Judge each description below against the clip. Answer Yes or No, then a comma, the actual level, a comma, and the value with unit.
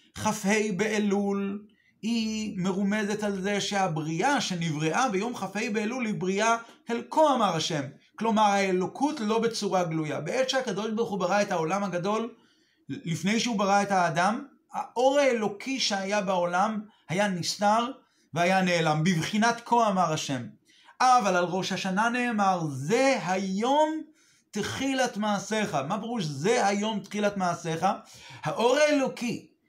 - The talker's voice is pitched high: Yes, high, 210 Hz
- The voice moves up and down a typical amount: Yes, average, 3.9 semitones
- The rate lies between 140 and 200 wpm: No, average, 130 wpm